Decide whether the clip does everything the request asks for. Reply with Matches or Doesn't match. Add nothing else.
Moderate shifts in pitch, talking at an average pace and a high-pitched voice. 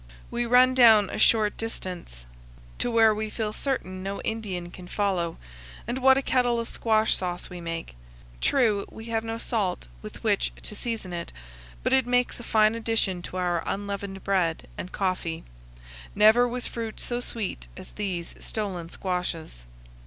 Matches